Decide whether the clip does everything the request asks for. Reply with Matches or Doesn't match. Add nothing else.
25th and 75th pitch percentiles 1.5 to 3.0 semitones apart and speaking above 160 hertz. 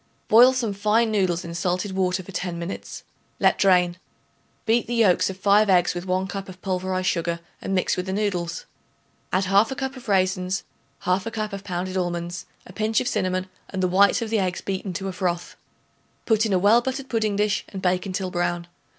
Matches